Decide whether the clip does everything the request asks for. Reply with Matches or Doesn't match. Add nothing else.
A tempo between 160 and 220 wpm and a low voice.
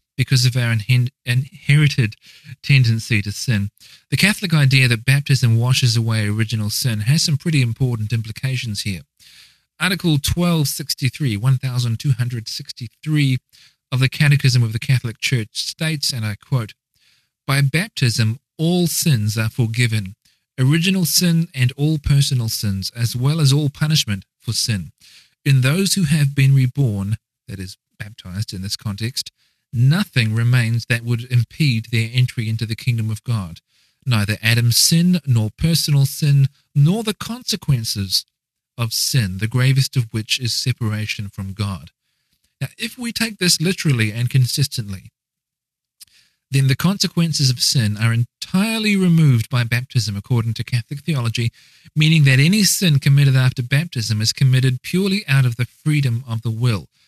Doesn't match